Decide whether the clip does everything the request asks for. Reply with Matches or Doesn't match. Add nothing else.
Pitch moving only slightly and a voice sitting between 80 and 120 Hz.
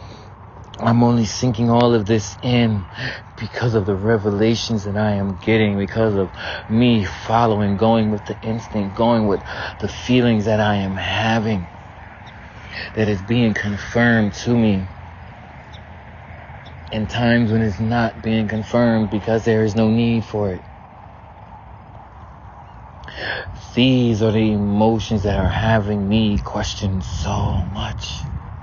Matches